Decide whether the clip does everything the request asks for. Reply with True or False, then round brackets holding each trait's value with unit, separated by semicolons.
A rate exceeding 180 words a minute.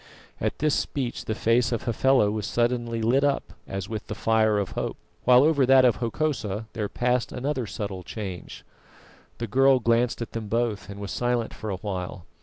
True (190 wpm)